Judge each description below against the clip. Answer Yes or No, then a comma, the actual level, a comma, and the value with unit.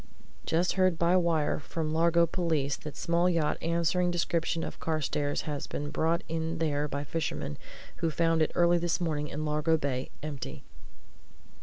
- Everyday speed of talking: Yes, average, 160 wpm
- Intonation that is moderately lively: No, narrow, 2.1 semitones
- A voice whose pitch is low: No, medium, 160 Hz